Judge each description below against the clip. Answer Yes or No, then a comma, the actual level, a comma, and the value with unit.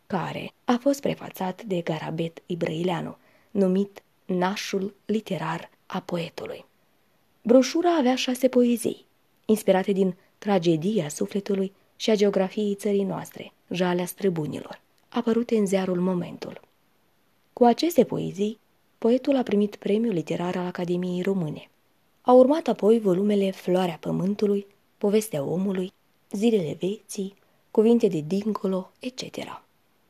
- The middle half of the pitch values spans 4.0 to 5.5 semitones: No, average, 3.3 semitones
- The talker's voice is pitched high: Yes, high, 200 Hz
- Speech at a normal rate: No, slow, 110 wpm